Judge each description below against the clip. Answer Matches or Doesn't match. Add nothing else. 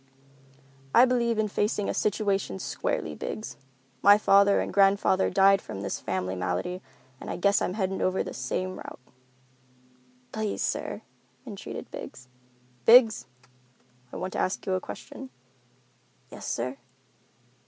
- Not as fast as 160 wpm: Matches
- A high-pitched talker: Matches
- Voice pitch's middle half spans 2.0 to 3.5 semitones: Matches